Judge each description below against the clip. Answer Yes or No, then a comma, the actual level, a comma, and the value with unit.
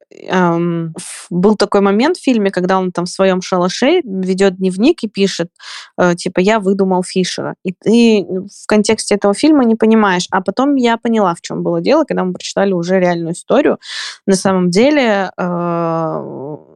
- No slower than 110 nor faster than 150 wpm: No, fast, 160 wpm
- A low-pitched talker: No, high, 195 Hz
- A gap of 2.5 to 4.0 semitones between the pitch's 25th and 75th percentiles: Yes, average, 3.3 semitones